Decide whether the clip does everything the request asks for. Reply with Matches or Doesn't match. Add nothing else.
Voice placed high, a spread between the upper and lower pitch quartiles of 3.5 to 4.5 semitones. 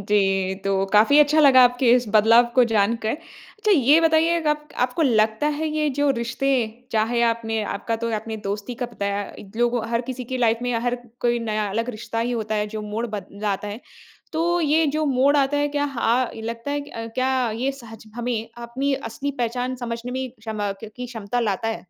Matches